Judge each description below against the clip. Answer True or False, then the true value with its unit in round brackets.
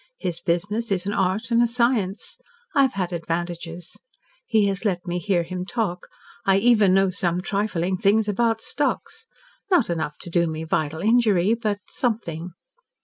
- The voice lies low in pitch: False (195 Hz)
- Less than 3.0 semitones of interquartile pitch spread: False (4.2 semitones)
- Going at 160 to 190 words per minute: True (165 wpm)